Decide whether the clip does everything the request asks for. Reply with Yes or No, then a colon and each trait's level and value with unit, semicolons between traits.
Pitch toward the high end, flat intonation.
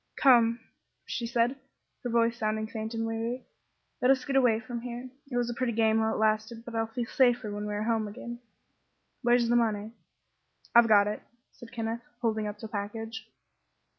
Yes: high, 230 Hz; narrow, 1.6 semitones